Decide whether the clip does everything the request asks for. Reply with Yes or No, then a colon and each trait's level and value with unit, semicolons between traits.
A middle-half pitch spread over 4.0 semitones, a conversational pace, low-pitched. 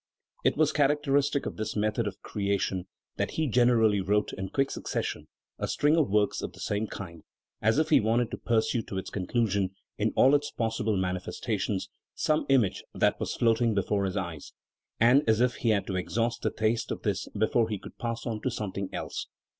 No: average, 3.5 semitones; average, 195 wpm; low, 110 Hz